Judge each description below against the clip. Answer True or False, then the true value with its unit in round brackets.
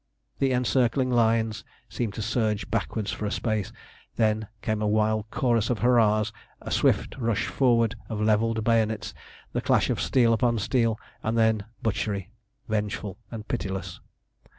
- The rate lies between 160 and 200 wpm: False (150 wpm)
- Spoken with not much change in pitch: True (1.6 semitones)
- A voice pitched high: False (110 Hz)